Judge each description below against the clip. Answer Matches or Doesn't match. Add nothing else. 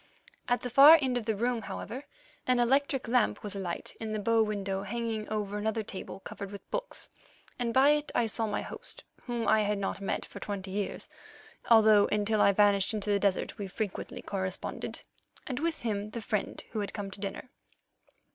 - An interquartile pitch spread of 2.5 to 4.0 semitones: Matches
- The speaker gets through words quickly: Doesn't match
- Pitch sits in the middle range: Doesn't match